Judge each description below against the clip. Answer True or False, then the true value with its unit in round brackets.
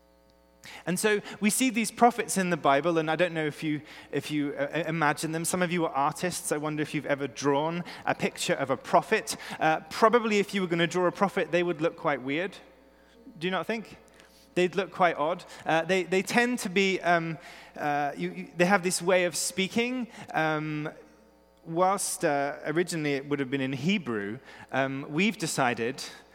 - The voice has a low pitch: False (170 Hz)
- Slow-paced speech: False (200 wpm)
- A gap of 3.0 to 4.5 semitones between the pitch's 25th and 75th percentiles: True (4.1 semitones)